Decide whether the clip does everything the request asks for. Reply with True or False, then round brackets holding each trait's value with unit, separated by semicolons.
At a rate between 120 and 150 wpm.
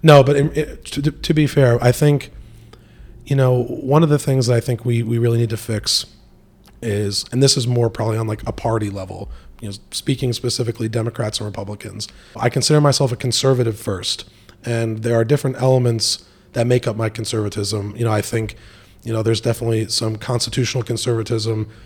False (190 wpm)